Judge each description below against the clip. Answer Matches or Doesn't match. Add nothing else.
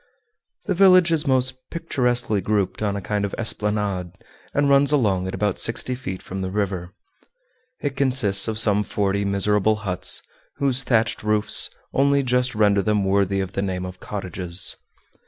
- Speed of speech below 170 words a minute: Matches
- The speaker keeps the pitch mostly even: Doesn't match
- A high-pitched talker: Doesn't match